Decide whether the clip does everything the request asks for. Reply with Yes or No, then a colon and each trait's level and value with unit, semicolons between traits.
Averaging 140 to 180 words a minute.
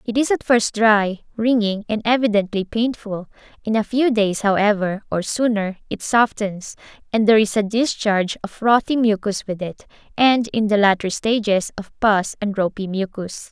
Yes: average, 170 wpm